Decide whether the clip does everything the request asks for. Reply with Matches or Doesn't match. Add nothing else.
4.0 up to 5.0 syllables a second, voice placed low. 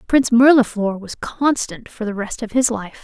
Doesn't match